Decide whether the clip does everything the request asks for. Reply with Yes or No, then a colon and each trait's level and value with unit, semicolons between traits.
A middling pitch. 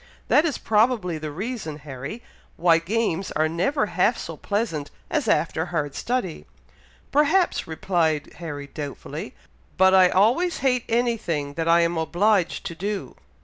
Yes: medium, 180 Hz